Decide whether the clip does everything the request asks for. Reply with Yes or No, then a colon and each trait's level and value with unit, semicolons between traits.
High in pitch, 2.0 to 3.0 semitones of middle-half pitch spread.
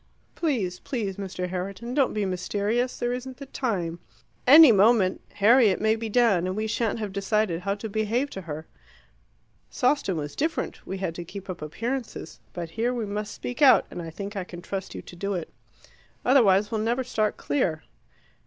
No: high, 210 Hz; average, 4.6 semitones